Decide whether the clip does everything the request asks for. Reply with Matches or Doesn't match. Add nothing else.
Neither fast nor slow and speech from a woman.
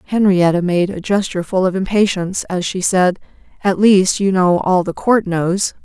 Matches